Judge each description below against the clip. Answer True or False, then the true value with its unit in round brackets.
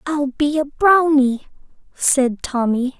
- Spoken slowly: True (120 wpm)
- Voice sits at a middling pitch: False (280 Hz)